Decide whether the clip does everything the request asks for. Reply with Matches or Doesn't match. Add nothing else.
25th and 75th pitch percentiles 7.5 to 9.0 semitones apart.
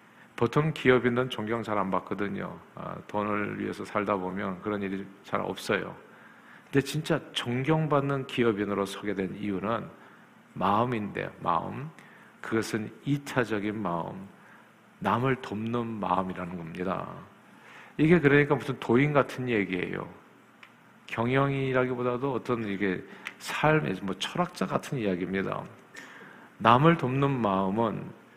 Doesn't match